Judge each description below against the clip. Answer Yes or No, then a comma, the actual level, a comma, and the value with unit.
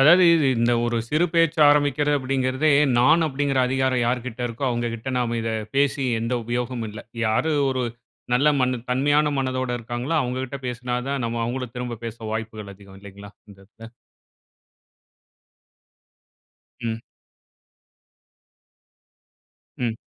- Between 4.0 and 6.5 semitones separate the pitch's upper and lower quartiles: No, average, 2.9 semitones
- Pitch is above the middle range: No, low, 125 Hz